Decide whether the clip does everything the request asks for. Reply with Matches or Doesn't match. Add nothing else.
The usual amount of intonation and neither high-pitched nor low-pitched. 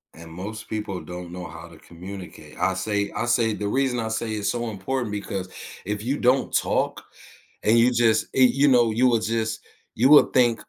Doesn't match